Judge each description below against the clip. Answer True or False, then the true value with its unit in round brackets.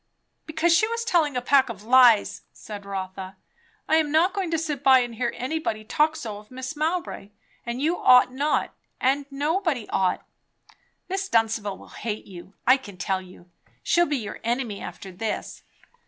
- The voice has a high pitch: True (255 Hz)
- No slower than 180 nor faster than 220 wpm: False (170 wpm)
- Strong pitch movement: True (6.8 semitones)